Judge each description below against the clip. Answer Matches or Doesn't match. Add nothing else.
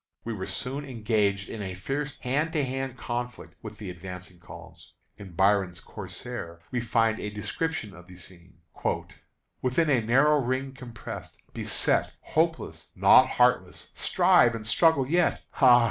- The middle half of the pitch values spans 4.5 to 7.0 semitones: Matches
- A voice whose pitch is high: Doesn't match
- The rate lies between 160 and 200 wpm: Doesn't match